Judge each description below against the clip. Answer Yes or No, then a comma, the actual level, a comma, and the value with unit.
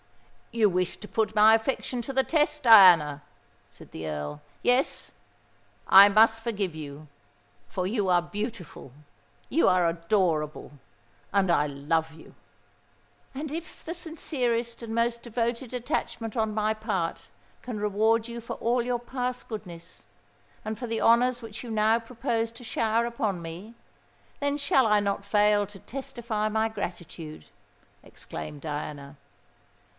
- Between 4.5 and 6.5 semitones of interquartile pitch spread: Yes, wide, 5.5 semitones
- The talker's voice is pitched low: No, high, 215 Hz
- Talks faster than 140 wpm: No, slow, 135 wpm